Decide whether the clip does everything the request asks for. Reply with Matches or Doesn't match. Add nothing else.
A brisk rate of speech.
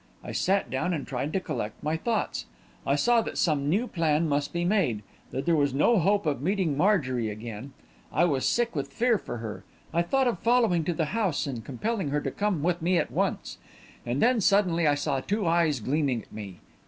Matches